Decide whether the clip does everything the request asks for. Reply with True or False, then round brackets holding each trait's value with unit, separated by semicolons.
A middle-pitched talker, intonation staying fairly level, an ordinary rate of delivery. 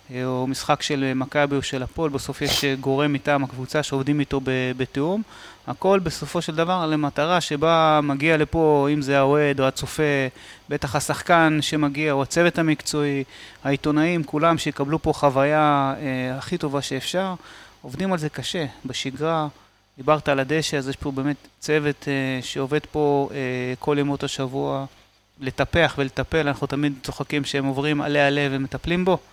False (145 Hz; 2.1 semitones; 155 wpm)